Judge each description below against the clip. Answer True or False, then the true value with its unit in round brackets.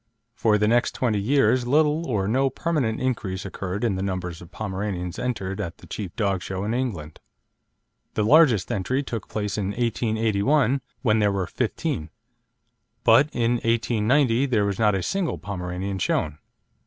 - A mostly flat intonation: False (4.4 semitones)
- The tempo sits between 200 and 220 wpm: False (160 wpm)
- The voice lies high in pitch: False (105 Hz)